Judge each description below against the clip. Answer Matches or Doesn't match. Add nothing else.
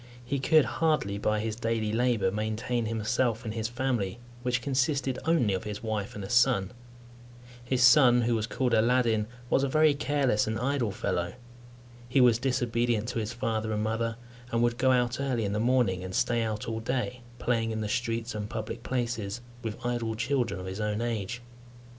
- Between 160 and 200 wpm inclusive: Matches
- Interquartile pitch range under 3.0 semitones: Matches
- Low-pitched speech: Matches